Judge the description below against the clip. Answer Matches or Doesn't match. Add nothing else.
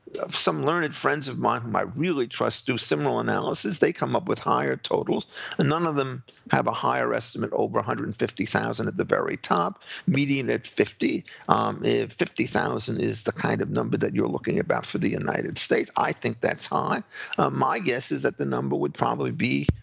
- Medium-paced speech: Doesn't match